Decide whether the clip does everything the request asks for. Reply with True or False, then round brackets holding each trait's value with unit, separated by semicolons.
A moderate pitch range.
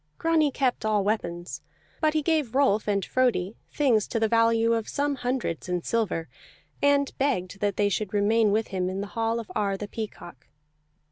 True (4.4 semitones)